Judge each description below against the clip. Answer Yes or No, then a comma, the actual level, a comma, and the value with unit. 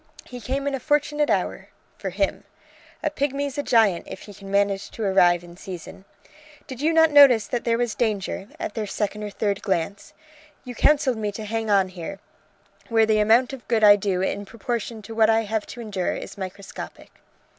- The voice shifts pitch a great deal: No, average, 3.8 semitones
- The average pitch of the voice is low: No, high, 220 Hz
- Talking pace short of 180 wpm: No, average, 200 wpm